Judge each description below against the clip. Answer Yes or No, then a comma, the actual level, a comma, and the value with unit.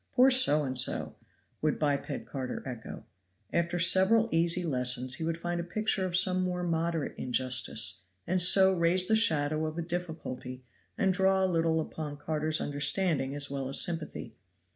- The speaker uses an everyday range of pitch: Yes, average, 4.2 semitones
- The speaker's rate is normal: Yes, average, 170 wpm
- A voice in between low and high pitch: Yes, medium, 165 Hz